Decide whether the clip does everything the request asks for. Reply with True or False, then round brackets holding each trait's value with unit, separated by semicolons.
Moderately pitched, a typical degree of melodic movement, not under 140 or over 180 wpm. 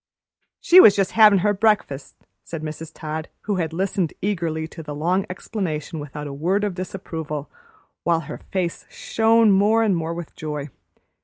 True (170 Hz; 4.4 semitones; 165 wpm)